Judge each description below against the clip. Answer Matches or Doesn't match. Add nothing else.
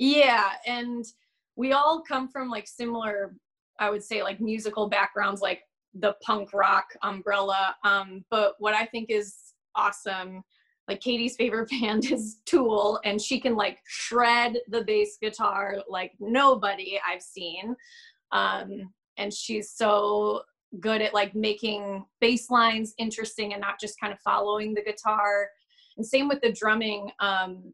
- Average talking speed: Matches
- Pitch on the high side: Matches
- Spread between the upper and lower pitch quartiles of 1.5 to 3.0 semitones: Matches